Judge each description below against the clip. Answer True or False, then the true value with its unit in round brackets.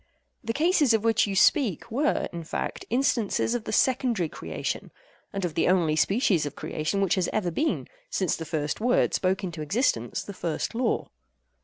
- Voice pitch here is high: True (195 Hz)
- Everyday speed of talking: True (175 wpm)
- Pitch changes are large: True (6.3 semitones)